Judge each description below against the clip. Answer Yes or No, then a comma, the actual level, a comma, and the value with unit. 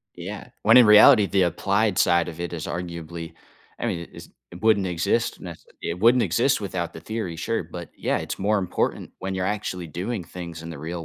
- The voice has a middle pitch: No, very low, 90 Hz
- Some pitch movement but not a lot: Yes, average, 3.7 semitones